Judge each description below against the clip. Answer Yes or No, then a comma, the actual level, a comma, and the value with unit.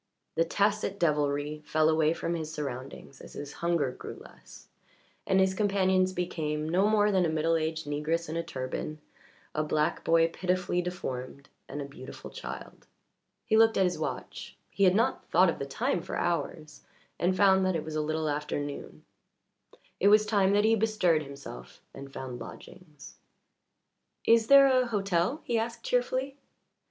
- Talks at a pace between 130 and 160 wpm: No, average, 170 wpm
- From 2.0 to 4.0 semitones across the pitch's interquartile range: No, average, 4.7 semitones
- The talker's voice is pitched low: No, medium, 170 Hz